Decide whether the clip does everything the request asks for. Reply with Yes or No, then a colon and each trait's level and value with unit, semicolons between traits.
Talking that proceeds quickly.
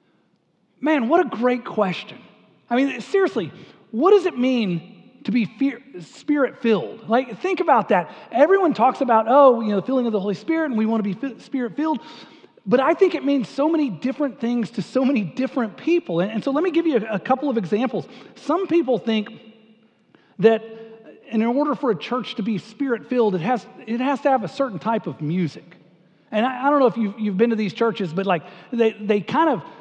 Yes: fast, 220 wpm